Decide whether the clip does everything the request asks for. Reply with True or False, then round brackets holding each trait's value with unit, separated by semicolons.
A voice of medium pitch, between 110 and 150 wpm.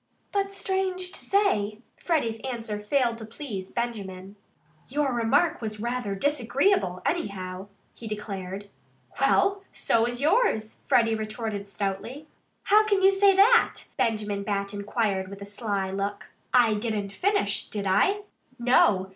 False (225 Hz; 140 wpm)